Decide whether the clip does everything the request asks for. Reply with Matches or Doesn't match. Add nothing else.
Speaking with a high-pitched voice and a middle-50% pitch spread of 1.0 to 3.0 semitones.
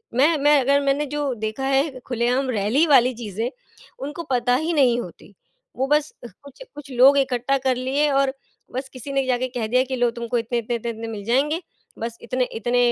Matches